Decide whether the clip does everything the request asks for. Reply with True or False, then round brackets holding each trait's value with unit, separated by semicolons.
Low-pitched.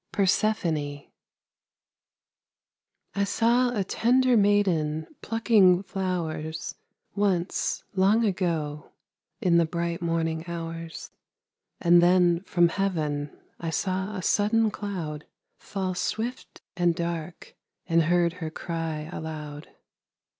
False (175 Hz)